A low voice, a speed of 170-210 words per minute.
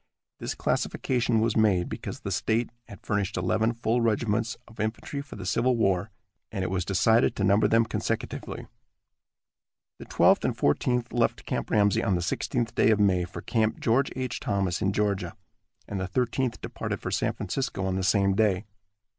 Yes: low, 110 Hz; average, 180 wpm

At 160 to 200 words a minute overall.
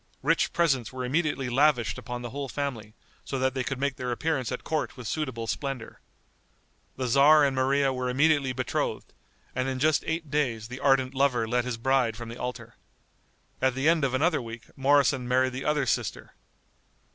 Yes: average, 185 wpm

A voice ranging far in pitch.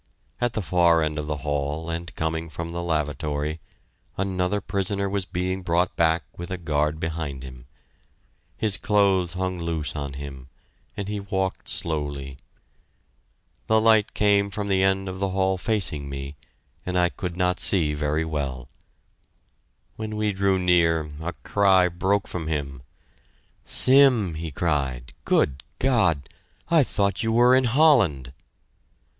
No: average, 4.6 semitones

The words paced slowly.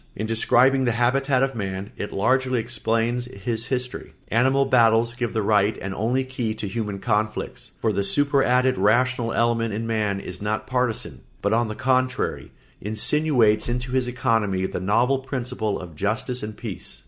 No: average, 165 wpm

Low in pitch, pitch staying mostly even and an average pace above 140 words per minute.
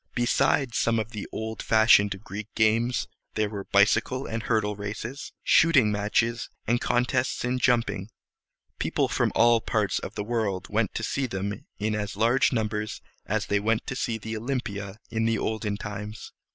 Yes: low, 110 Hz; narrow, 2.3 semitones; average, 160 wpm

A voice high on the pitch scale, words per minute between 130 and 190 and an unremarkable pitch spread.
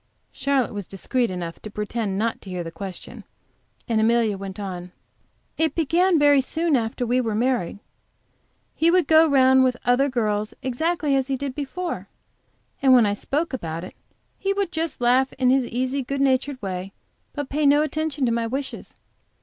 Yes: very high, 255 Hz; average, 180 wpm; average, 5.0 semitones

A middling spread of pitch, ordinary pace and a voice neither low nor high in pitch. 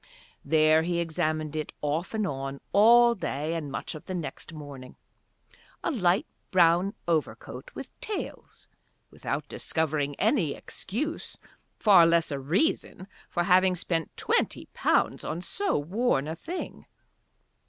No: average, 4.0 semitones; slow, 130 wpm; medium, 170 Hz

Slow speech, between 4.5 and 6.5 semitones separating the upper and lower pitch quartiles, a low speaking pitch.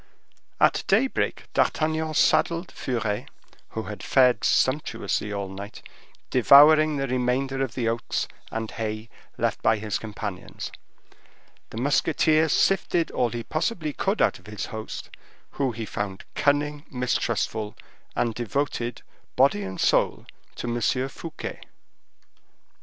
Yes: slow, 125 wpm; average, 5.1 semitones; low, 125 Hz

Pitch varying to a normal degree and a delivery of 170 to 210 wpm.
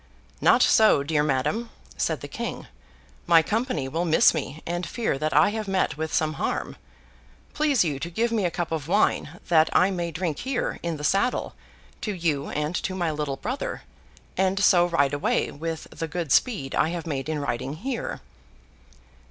Yes: average, 4.2 semitones; average, 185 wpm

